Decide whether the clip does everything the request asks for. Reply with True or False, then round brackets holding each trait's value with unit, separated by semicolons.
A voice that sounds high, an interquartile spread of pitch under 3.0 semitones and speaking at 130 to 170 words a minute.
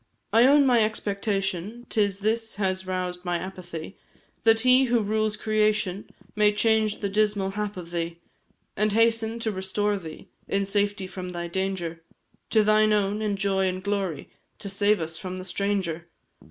True (200 Hz; 2.4 semitones; 165 wpm)